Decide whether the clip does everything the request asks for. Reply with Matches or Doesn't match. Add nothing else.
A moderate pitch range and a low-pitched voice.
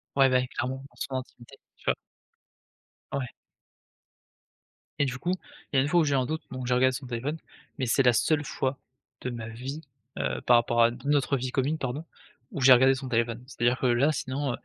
Doesn't match